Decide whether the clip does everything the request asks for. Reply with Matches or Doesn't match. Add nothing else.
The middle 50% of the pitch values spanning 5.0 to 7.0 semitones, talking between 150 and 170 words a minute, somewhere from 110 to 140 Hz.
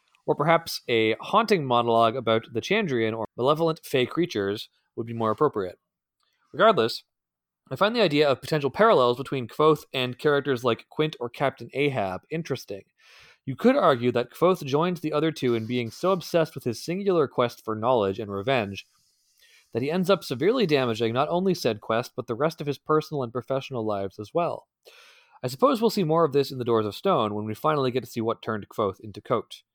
Doesn't match